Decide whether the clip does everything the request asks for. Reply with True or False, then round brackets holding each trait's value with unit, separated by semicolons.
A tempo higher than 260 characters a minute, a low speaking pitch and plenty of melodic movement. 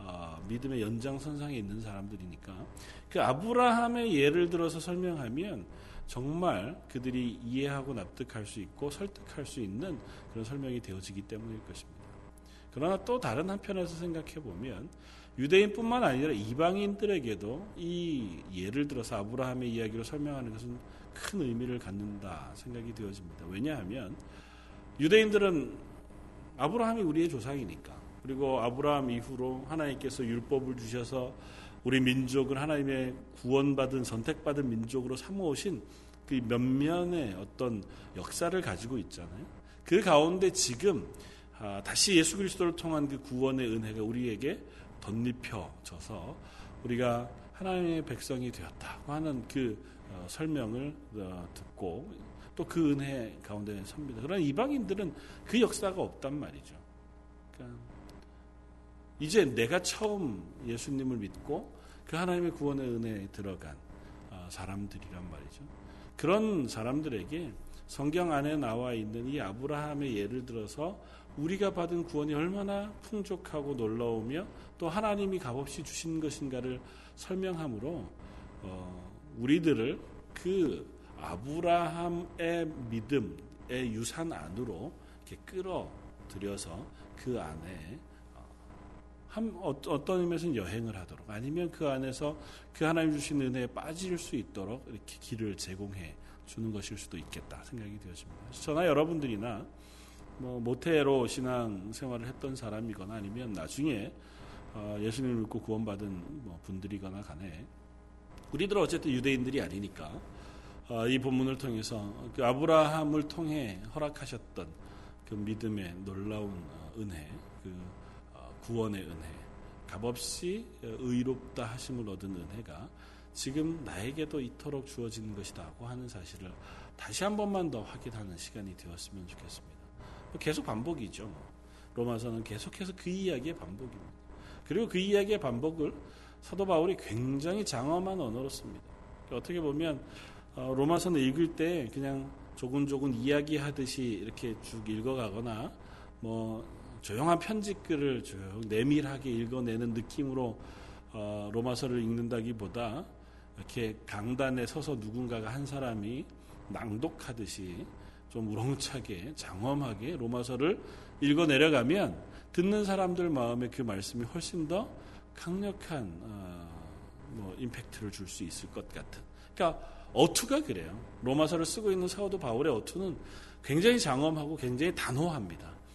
True (300 characters per minute; 125 Hz; 6.8 semitones)